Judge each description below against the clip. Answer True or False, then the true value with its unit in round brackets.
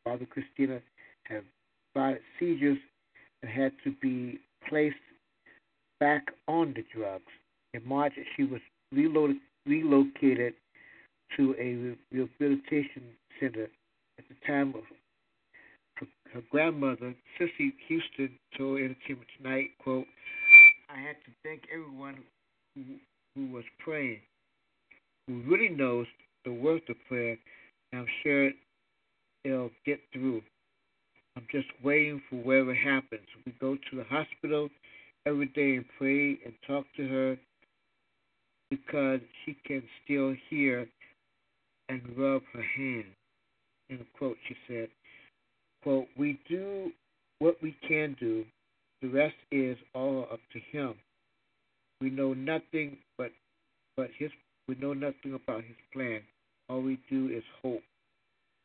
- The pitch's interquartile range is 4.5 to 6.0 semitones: False (2.6 semitones)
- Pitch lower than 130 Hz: False (135 Hz)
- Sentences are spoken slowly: True (125 wpm)